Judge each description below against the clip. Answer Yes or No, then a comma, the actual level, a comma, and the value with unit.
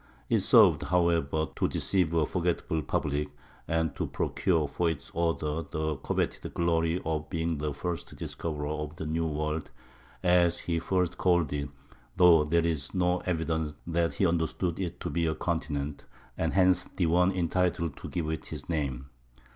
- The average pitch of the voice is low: Yes, very low, 80 Hz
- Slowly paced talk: No, average, 165 wpm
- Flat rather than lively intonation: Yes, narrow, 2.2 semitones